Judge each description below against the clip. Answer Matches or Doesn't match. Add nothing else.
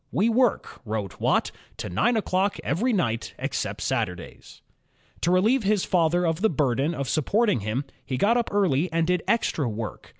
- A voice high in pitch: Doesn't match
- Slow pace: Doesn't match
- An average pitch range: Doesn't match